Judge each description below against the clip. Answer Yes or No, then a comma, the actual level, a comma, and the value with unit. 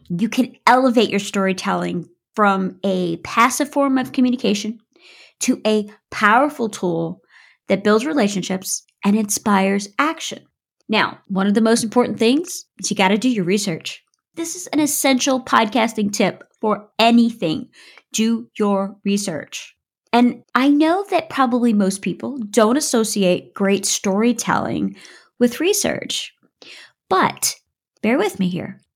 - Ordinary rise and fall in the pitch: Yes, average, 4.3 semitones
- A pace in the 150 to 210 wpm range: No, slow, 135 wpm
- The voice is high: Yes, high, 220 Hz